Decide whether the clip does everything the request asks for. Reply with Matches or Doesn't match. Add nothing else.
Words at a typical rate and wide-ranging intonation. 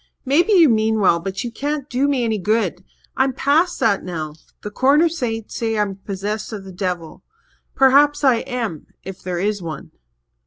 Matches